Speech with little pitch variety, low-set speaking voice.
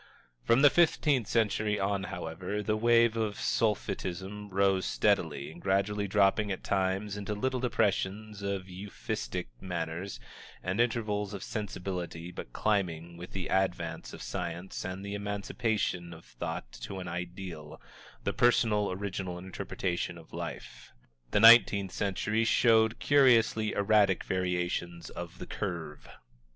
No: average, 3.0 semitones; low, 100 Hz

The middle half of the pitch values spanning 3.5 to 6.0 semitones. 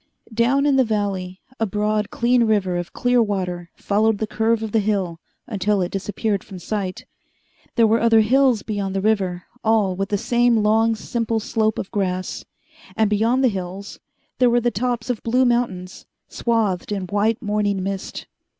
No: average, 2.8 semitones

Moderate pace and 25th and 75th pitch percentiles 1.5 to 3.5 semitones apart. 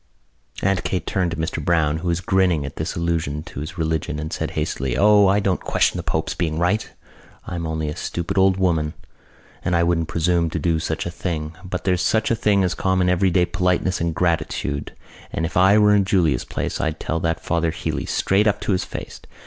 No: fast, 215 wpm; average, 2.8 semitones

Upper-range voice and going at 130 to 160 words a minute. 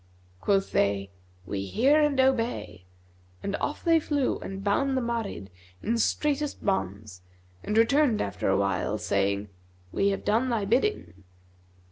Yes: high, 200 Hz; average, 140 wpm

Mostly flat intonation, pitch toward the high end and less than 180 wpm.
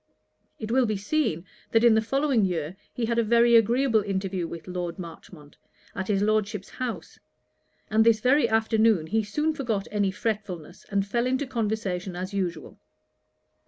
No: average, 3.7 semitones; high, 215 Hz; average, 160 wpm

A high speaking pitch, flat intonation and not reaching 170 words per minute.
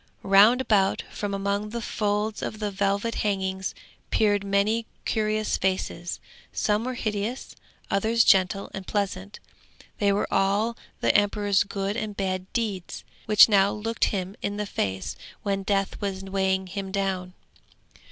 Yes: high, 200 Hz; narrow, 1.6 semitones; average, 140 wpm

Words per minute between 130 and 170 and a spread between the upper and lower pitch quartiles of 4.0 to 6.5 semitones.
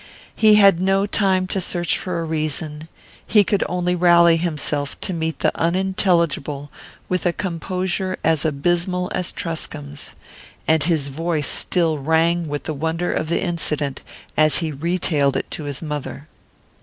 No: average, 155 wpm; average, 2.9 semitones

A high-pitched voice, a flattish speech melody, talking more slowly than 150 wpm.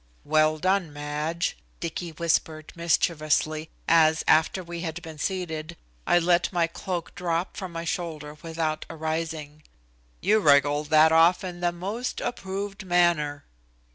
No: medium, 165 Hz; narrow, 2.2 semitones; slow, 135 wpm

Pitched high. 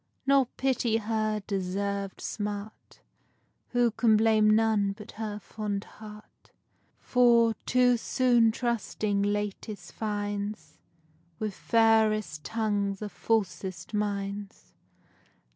Yes: high, 215 Hz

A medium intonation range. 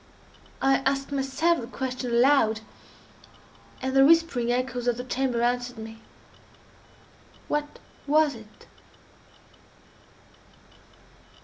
No: narrow, 2.3 semitones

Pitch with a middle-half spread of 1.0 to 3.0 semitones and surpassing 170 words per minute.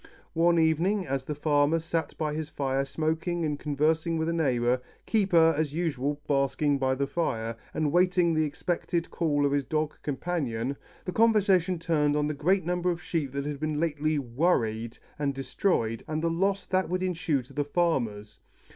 No: average, 3.5 semitones; average, 180 wpm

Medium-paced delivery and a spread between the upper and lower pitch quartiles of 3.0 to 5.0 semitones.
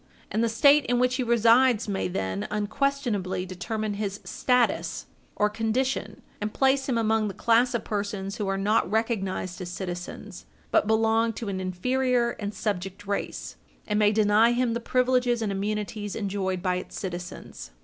Yes: average, 165 wpm; average, 3.4 semitones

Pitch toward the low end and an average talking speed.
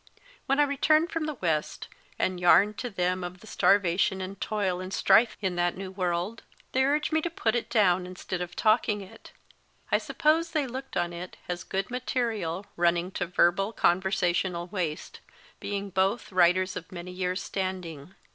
No: high, 190 Hz; average, 170 wpm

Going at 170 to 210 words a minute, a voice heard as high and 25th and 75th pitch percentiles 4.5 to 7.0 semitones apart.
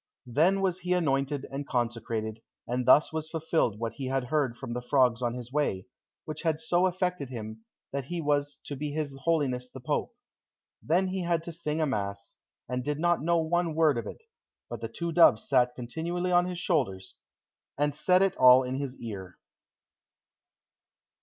No: average, 185 wpm; medium, 145 Hz; average, 5.2 semitones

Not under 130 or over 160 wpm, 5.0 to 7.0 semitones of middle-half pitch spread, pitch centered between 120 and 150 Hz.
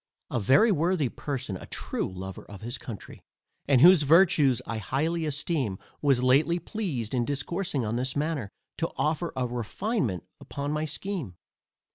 Yes: average, 155 wpm; wide, 5.6 semitones; medium, 140 Hz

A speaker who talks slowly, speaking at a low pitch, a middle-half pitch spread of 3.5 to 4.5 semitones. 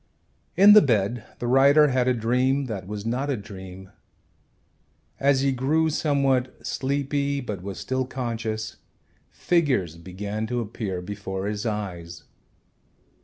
No: slow, 130 wpm; low, 120 Hz; average, 5.3 semitones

